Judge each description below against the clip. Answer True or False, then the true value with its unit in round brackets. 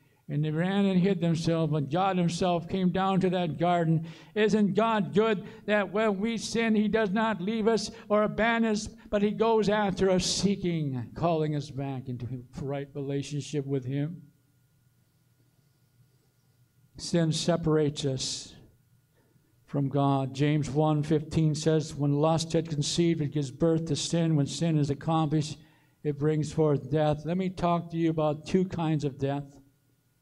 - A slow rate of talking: False (155 wpm)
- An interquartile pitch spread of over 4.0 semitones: True (4.7 semitones)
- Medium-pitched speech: True (155 Hz)